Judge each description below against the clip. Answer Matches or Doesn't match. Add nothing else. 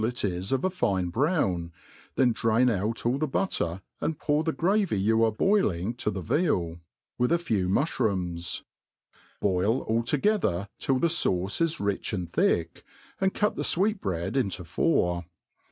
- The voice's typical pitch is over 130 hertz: Doesn't match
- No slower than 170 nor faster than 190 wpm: Doesn't match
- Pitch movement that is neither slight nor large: Doesn't match